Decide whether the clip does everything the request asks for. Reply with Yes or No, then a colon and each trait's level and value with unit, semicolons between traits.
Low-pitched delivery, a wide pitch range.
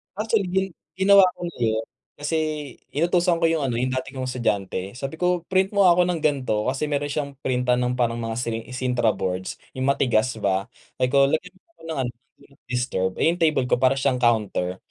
Yes: low, 130 Hz; wide, 5.7 semitones